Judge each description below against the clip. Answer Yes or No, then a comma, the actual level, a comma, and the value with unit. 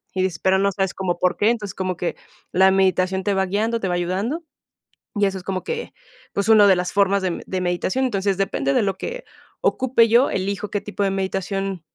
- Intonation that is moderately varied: No, narrow, 1.7 semitones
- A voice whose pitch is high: Yes, high, 195 Hz